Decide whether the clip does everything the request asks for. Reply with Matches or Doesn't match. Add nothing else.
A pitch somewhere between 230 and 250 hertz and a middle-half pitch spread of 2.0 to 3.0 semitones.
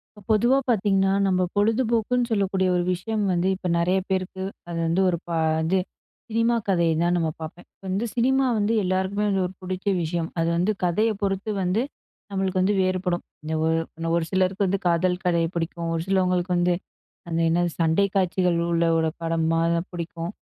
Doesn't match